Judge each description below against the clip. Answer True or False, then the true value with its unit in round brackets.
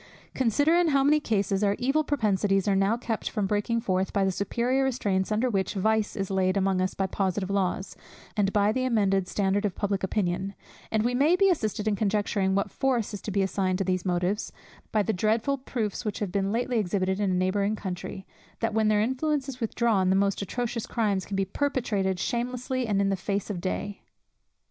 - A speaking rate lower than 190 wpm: False (205 wpm)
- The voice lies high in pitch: True (205 Hz)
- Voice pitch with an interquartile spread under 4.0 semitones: True (3.4 semitones)